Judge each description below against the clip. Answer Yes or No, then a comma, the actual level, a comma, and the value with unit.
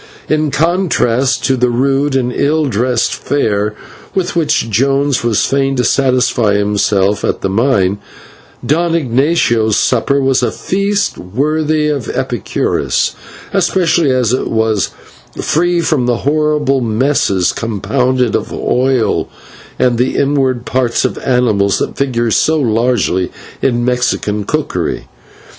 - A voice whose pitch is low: Yes, low, 130 Hz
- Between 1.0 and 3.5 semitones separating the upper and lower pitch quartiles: No, average, 4.1 semitones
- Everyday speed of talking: No, slow, 125 wpm